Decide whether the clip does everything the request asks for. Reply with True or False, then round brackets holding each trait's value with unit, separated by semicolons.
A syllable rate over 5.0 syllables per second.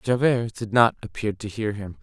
False (4.9 syllables/s)